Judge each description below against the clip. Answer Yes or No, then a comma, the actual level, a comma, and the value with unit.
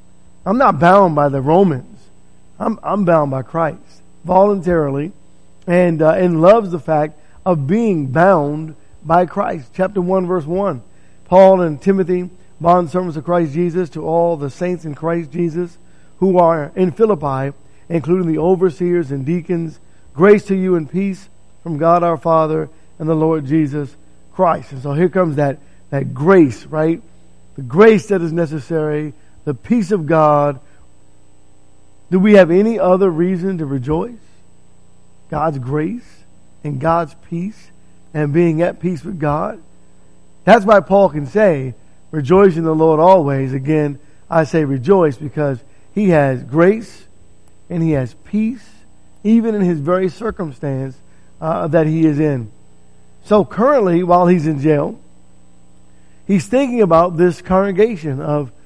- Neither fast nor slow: Yes, average, 150 wpm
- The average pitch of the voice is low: No, medium, 165 Hz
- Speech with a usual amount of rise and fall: Yes, average, 4.2 semitones